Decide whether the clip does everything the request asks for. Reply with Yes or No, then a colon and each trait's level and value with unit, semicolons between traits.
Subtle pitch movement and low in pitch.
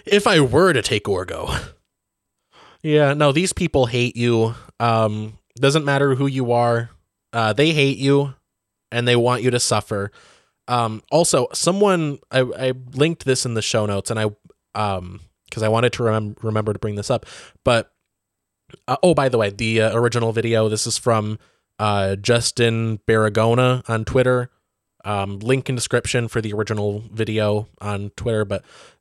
No: average, 3.0 semitones; low, 115 Hz